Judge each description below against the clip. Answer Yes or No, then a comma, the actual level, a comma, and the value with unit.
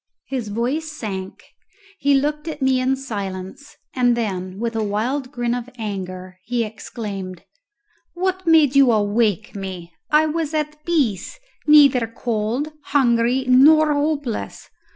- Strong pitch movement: Yes, wide, 5.7 semitones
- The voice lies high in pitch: Yes, high, 245 Hz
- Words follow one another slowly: Yes, slow, 130 wpm